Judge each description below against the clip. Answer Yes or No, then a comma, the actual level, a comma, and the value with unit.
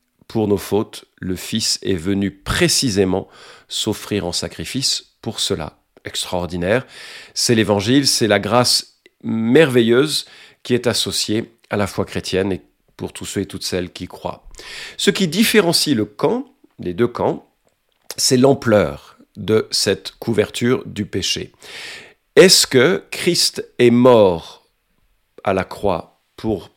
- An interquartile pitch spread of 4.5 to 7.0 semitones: Yes, average, 5.1 semitones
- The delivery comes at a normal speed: No, slow, 135 wpm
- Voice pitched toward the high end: No, low, 110 Hz